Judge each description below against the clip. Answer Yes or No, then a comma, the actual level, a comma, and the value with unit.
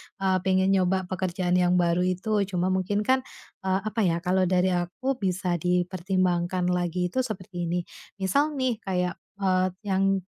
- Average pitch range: No, narrow, 1.5 semitones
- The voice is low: No, medium, 185 Hz